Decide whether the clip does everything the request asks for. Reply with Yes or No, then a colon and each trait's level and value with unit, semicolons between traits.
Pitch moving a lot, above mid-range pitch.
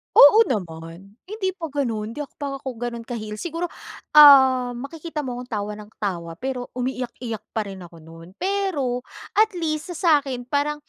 Yes: wide, 5.9 semitones; very high, 255 Hz